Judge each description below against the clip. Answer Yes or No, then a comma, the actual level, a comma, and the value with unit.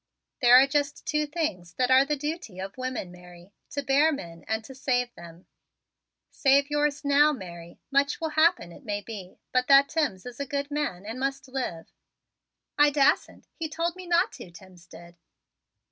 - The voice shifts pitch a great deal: Yes, wide, 7.5 semitones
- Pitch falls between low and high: No, very high, 270 Hz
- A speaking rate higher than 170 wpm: Yes, average, 180 wpm